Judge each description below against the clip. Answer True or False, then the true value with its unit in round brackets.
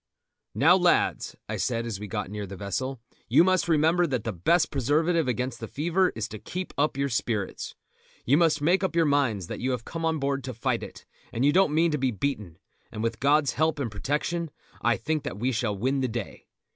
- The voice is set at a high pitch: False (135 Hz)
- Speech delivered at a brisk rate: True (220 wpm)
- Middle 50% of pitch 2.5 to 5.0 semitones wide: False (5.6 semitones)